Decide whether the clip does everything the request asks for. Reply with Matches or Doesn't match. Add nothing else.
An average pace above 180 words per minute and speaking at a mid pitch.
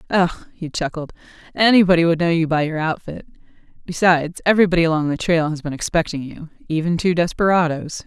Doesn't match